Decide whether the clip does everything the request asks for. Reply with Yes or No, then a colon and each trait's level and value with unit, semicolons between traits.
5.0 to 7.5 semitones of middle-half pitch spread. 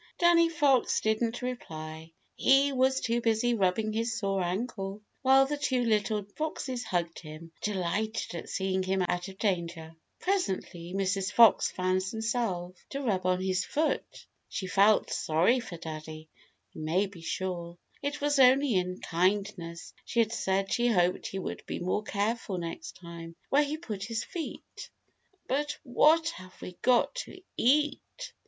Yes: wide, 5.6 semitones